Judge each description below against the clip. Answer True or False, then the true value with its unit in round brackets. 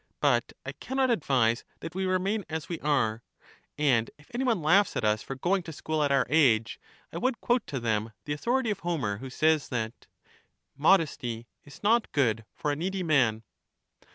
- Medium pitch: True (150 Hz)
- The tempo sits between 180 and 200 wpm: True (190 wpm)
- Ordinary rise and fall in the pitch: False (7.7 semitones)